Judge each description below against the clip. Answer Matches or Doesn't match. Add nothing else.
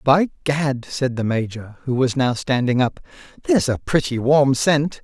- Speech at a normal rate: Matches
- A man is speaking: Matches